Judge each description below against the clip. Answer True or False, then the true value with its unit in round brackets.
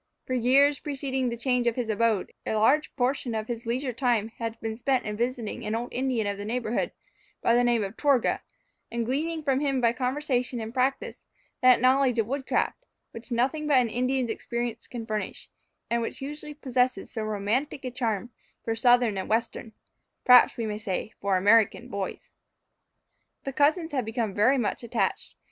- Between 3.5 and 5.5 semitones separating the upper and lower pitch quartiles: False (2.8 semitones)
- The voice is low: False (245 Hz)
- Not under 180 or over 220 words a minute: True (185 wpm)